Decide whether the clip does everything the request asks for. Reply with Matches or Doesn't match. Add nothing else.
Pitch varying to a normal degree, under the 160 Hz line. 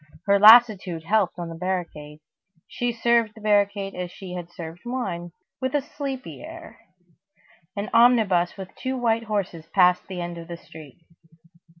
Doesn't match